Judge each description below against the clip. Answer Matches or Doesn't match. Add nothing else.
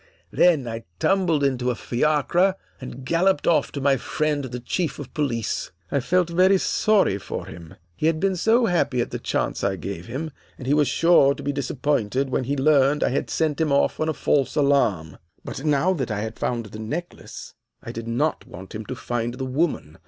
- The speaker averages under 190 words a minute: Doesn't match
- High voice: Doesn't match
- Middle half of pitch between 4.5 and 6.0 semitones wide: Matches